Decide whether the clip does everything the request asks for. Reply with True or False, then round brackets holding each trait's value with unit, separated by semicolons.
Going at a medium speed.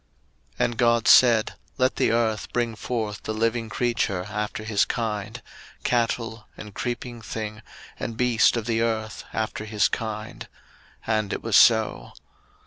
True (145 wpm)